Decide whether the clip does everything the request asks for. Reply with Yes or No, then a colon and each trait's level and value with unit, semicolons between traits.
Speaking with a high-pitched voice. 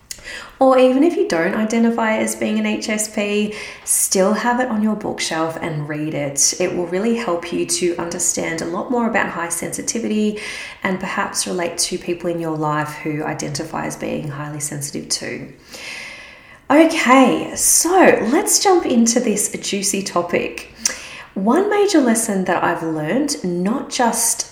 Yes: high, 200 Hz